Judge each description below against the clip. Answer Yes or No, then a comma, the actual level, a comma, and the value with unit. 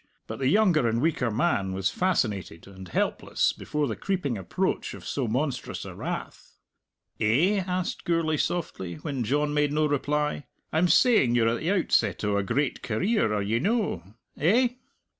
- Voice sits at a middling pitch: Yes, medium, 145 Hz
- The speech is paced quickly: No, average, 165 wpm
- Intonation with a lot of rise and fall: Yes, wide, 7.5 semitones